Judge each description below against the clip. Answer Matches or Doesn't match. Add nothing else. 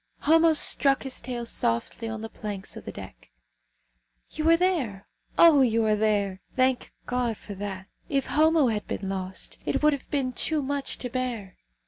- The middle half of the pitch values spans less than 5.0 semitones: Doesn't match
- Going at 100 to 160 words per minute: Doesn't match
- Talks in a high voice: Matches